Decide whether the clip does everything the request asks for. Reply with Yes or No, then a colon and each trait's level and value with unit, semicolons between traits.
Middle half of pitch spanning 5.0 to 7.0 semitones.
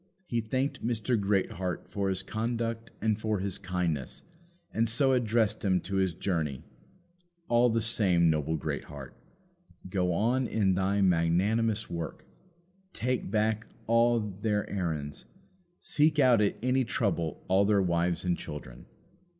No: average, 4.4 semitones